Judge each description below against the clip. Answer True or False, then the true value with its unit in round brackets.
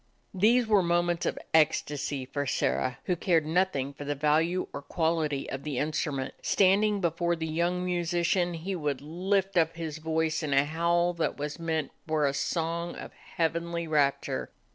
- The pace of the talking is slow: False (170 wpm)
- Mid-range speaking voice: True (165 Hz)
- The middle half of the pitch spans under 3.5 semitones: True (2.7 semitones)